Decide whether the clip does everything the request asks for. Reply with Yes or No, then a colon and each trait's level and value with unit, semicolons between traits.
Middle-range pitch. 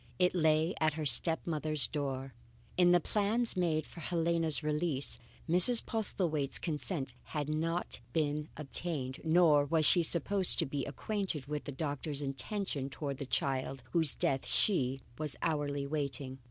Yes: medium, 155 Hz